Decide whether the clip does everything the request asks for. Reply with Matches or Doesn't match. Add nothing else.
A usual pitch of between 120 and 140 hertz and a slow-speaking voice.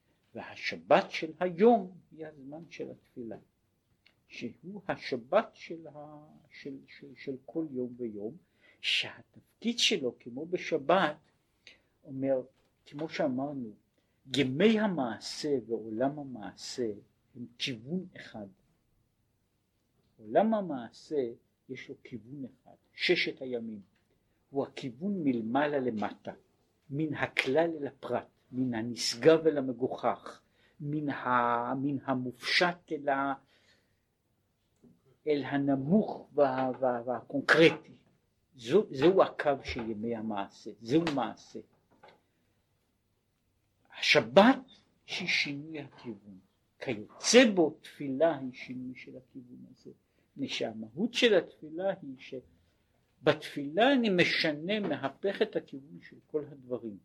Matches